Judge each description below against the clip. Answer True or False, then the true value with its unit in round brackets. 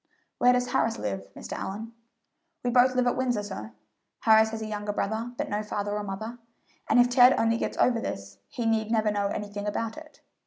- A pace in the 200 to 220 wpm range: True (205 wpm)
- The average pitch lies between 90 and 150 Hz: False (220 Hz)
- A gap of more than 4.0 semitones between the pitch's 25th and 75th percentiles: False (3.0 semitones)